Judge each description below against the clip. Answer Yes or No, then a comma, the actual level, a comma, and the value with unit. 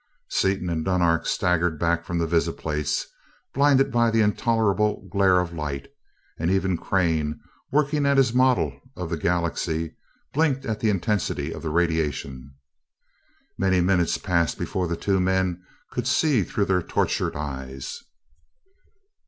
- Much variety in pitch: No, average, 4.4 semitones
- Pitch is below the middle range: Yes, very low, 90 Hz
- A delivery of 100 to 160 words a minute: Yes, average, 140 wpm